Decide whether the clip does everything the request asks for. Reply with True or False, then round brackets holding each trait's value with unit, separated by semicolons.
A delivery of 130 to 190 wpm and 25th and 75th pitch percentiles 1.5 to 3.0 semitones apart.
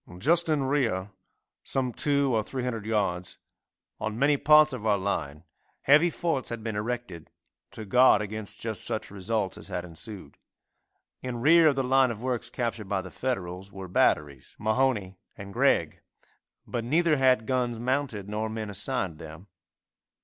False (160 wpm; 4.8 semitones)